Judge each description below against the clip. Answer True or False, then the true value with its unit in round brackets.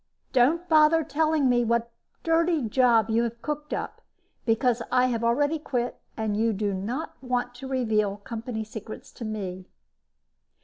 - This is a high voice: True (240 Hz)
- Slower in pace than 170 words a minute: True (150 wpm)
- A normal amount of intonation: True (4.4 semitones)